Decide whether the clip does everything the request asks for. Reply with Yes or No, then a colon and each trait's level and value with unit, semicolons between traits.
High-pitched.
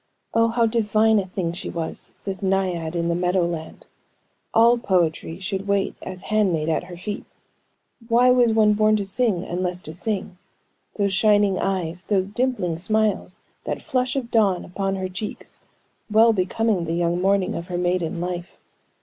Yes: high, 195 Hz